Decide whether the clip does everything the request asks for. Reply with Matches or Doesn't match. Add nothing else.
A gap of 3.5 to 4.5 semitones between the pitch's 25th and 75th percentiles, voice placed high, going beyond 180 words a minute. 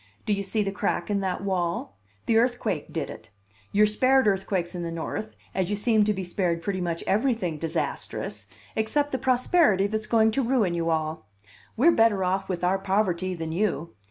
Matches